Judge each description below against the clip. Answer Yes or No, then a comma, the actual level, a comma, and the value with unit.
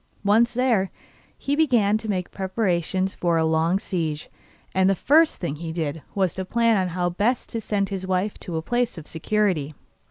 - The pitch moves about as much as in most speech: Yes, average, 4.2 semitones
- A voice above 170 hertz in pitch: Yes, high, 190 Hz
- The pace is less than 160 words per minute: No, average, 185 wpm